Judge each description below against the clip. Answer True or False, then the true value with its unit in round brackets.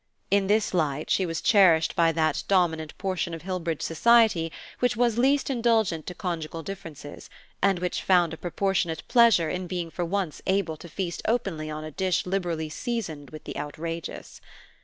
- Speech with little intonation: False (3.5 semitones)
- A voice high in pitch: False (175 Hz)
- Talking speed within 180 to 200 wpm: False (170 wpm)